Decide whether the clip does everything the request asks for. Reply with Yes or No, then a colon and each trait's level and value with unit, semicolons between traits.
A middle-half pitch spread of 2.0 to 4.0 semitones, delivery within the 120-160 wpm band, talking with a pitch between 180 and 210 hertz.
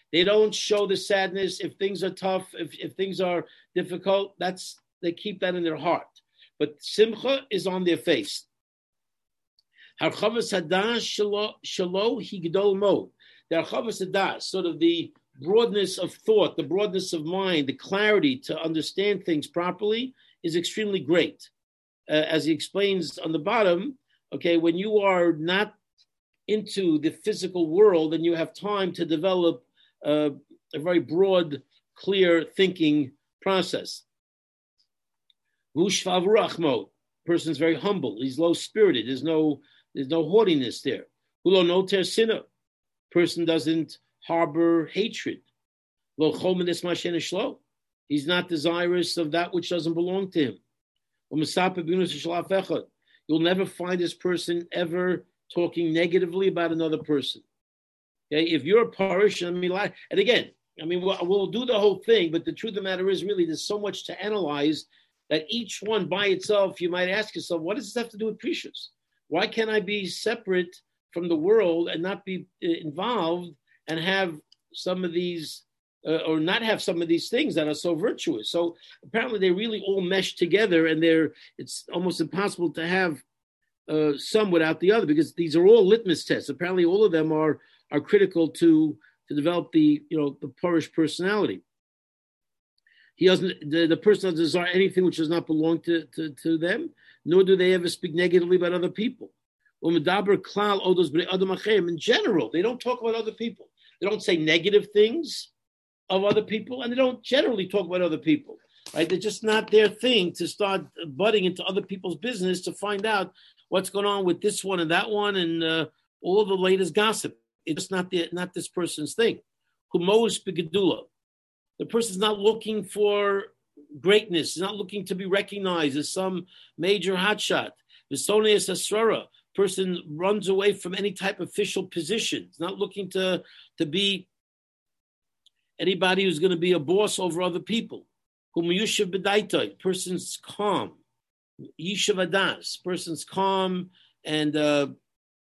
Yes: average, 3.6 semitones; average, 155 wpm; medium, 185 Hz